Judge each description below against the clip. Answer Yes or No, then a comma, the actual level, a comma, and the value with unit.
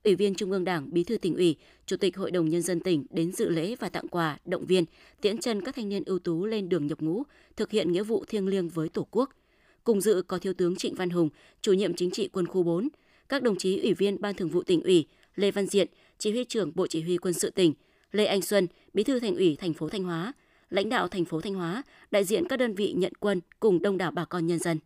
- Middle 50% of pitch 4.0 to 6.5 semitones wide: No, average, 3.5 semitones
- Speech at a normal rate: No, fast, 270 wpm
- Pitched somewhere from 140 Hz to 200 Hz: Yes, high, 190 Hz